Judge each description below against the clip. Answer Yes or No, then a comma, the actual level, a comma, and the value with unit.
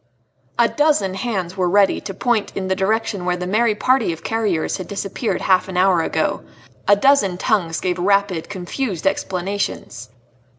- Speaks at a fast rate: No, average, 165 wpm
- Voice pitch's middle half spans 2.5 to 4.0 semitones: Yes, average, 3.0 semitones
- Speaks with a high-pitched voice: Yes, high, 195 Hz